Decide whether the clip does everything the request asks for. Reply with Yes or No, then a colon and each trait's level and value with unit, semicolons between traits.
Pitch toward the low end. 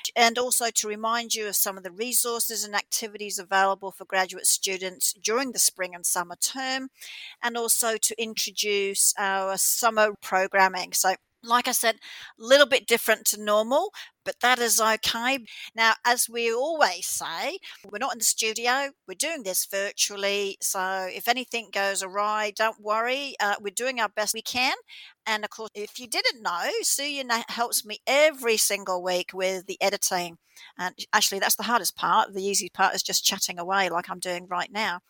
No: high, 215 Hz